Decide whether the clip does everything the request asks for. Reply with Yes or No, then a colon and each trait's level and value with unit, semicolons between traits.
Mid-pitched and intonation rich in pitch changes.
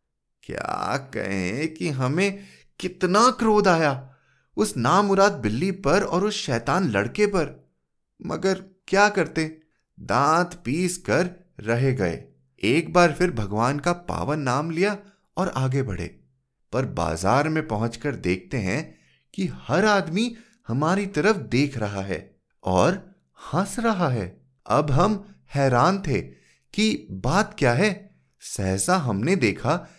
Yes: medium, 160 Hz; wide, 7.9 semitones